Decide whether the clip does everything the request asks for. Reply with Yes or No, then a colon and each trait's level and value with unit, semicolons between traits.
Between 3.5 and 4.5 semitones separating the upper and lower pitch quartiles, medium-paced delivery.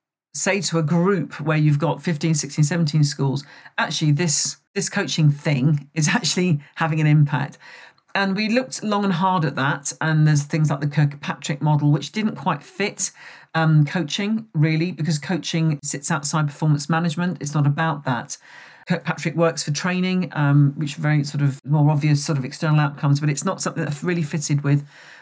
No: average, 3.1 semitones; average, 185 wpm